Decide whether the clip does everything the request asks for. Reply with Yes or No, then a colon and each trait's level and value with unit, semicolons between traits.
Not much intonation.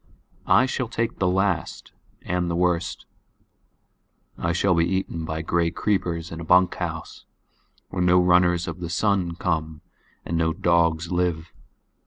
Yes: narrow, 1.5 semitones